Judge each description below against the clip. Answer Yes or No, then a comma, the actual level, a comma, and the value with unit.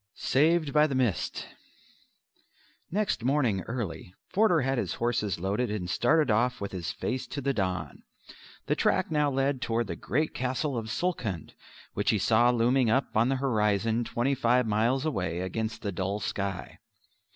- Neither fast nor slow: Yes, average, 165 wpm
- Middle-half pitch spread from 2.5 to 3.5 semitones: No, average, 4.7 semitones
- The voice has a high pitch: No, low, 120 Hz